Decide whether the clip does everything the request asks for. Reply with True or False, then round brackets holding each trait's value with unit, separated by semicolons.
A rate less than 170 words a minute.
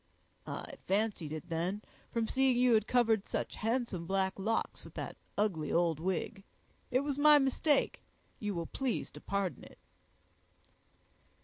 True (145 wpm)